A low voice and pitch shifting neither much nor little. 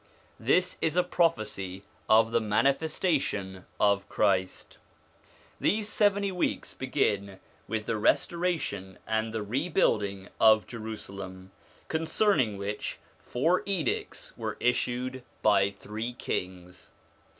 No: low, 110 Hz; wide, 8.0 semitones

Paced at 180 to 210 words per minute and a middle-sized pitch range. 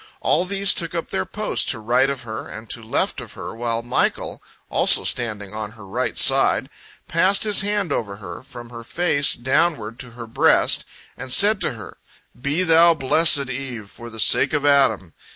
No: average, 190 wpm; wide, 6.4 semitones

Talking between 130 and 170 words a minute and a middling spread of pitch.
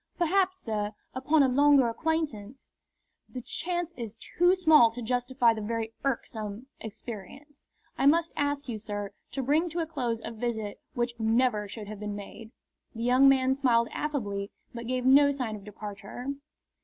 Yes: average, 165 wpm; average, 4.6 semitones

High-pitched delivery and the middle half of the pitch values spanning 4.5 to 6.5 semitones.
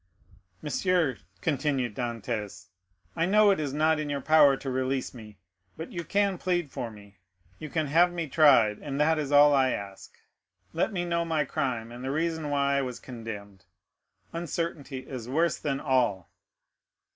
No: medium, 140 Hz; average, 5.0 semitones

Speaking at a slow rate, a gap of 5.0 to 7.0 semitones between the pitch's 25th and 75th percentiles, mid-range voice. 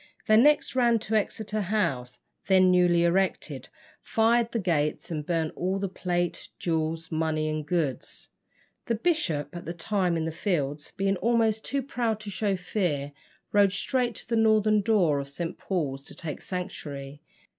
No: average, 165 wpm; average, 5.3 semitones; medium, 180 Hz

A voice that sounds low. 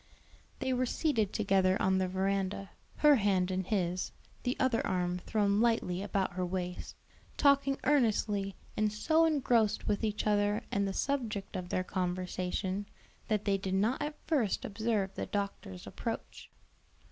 No: high, 200 Hz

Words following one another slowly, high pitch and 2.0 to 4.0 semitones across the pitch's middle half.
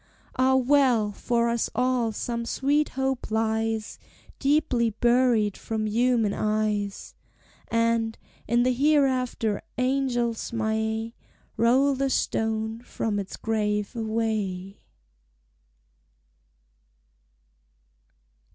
Yes: slow, 85 wpm; high, 230 Hz; narrow, 2.6 semitones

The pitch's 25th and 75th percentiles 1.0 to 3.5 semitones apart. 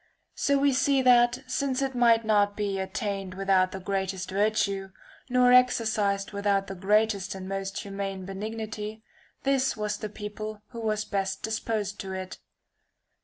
Yes: average, 2.8 semitones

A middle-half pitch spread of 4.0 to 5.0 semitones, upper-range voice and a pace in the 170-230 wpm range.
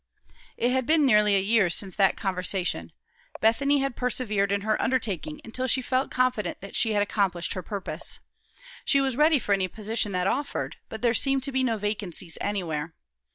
Yes: average, 4.7 semitones; high, 220 Hz; average, 185 wpm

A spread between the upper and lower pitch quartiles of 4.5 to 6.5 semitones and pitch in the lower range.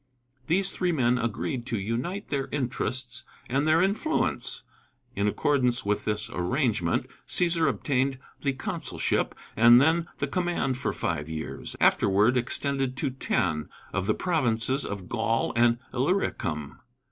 Yes: average, 4.8 semitones; low, 125 Hz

